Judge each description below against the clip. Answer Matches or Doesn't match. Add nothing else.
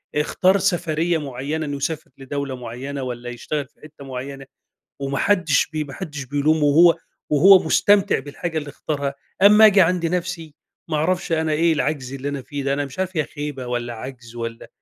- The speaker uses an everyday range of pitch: Matches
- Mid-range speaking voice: Matches